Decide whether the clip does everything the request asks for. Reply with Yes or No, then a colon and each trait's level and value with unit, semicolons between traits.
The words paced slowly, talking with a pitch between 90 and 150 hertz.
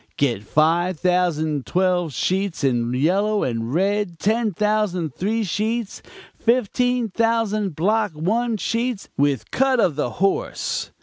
No: slow, 125 wpm; high, 190 Hz